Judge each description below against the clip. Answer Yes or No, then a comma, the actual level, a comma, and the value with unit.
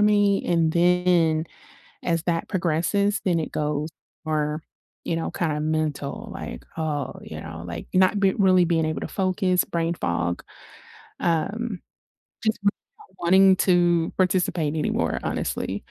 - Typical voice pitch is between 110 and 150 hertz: No, medium, 170 Hz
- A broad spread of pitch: No, average, 3.1 semitones